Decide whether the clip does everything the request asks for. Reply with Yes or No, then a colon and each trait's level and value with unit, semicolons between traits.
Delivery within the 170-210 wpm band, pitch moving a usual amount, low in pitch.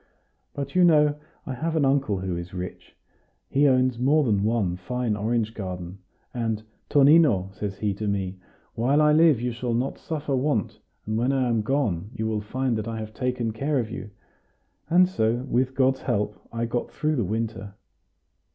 Yes: average, 185 wpm; average, 4.5 semitones; low, 120 Hz